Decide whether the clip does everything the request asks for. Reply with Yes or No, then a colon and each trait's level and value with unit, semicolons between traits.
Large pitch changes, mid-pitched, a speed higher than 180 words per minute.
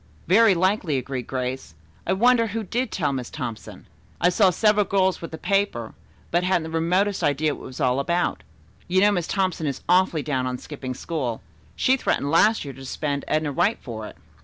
Yes: wide, 6.1 semitones; medium, 165 Hz; average, 200 wpm